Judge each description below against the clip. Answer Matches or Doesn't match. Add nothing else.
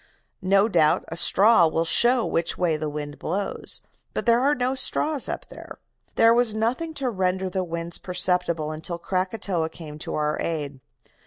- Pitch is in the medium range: Matches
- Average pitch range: Doesn't match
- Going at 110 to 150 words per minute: Doesn't match